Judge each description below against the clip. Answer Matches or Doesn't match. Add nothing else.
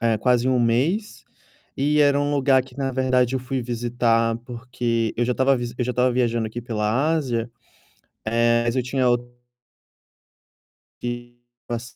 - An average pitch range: Doesn't match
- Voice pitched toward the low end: Matches